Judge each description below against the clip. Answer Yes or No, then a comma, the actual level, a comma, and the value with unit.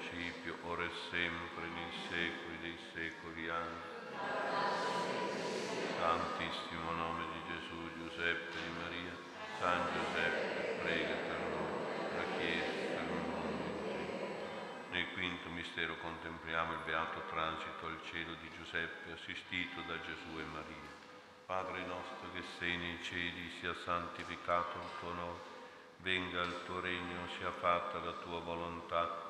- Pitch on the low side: Yes, very low, 85 Hz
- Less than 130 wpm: Yes, average, 120 wpm